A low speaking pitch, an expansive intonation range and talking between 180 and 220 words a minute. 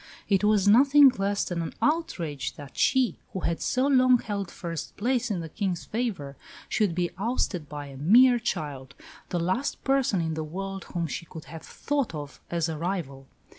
No: medium, 185 Hz; wide, 6.9 semitones; average, 185 wpm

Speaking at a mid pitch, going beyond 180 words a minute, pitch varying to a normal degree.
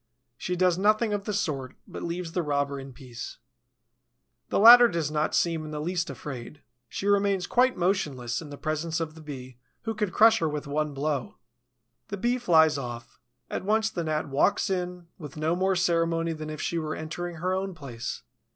Yes: medium, 165 Hz; average, 195 wpm; average, 4.0 semitones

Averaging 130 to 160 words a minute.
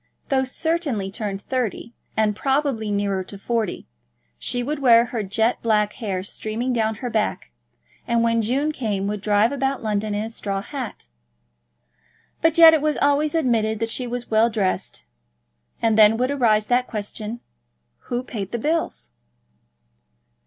Yes: average, 155 wpm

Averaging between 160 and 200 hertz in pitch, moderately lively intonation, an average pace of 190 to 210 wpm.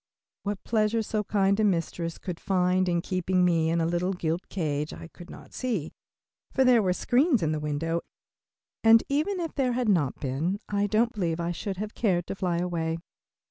Yes: medium, 185 Hz; average, 4.2 semitones; average, 195 wpm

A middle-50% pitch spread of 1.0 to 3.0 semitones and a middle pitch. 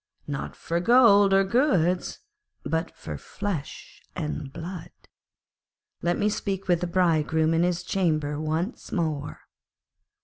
No: average, 3.7 semitones; medium, 175 Hz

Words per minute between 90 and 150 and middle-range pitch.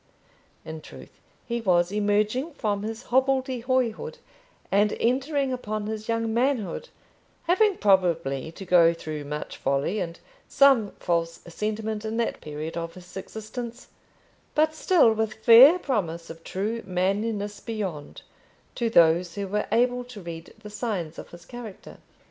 No: average, 140 wpm; high, 210 Hz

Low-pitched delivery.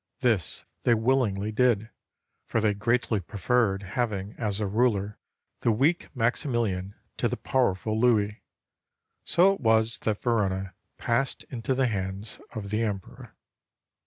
Yes: low, 110 Hz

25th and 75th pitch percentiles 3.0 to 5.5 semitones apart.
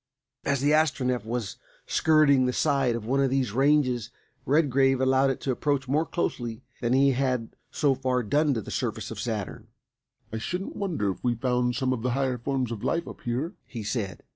No: narrow, 2.6 semitones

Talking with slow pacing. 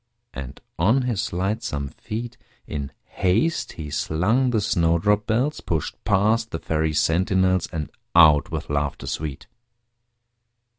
Yes: slow, 120 wpm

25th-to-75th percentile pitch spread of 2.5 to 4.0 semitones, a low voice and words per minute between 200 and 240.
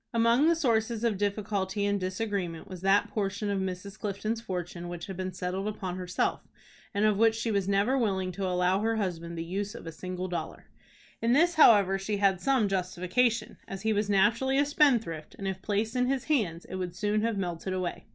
No: average, 3.3 semitones; high, 200 Hz; fast, 205 wpm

